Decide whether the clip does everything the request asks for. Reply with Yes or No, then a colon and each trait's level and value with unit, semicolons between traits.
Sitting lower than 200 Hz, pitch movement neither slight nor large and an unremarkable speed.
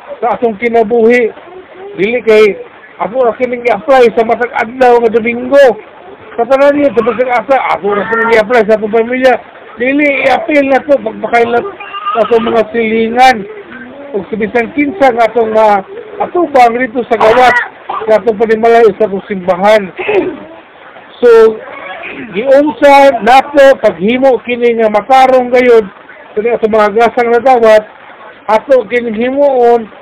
No: high, 240 Hz; average, 3.2 semitones; average, 135 wpm